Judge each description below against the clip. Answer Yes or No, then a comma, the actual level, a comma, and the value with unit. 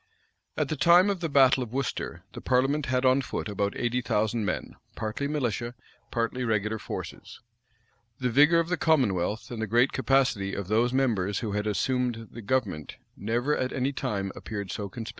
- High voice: No, low, 120 Hz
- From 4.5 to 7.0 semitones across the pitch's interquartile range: No, average, 4.1 semitones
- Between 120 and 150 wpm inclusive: No, average, 180 wpm